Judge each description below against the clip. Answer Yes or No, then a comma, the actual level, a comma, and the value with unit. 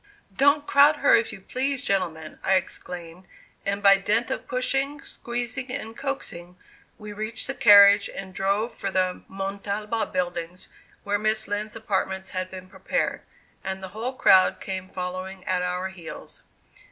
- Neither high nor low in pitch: No, high, 200 Hz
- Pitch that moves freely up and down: No, average, 3.5 semitones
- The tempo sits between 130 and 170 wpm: Yes, average, 155 wpm